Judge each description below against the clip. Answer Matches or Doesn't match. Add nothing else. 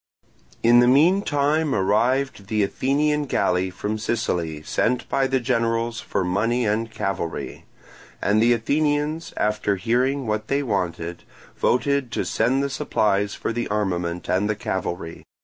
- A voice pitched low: Matches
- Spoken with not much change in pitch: Doesn't match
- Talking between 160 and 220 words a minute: Doesn't match